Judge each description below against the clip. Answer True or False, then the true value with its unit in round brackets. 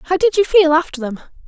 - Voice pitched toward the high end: True (330 Hz)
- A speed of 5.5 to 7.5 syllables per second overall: True (5.9 syllables/s)